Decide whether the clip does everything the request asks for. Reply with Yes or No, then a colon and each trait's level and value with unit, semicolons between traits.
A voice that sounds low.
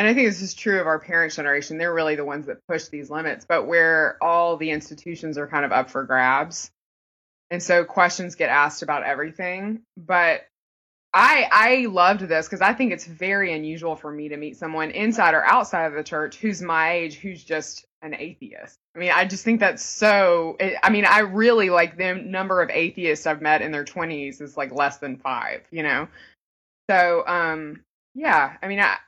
No: medium, 165 Hz